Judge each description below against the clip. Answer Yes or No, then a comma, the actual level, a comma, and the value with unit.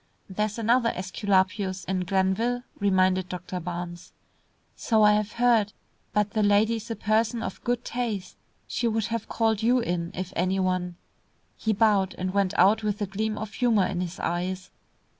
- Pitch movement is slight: No, average, 3.1 semitones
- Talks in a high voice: Yes, high, 205 Hz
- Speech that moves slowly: No, average, 175 wpm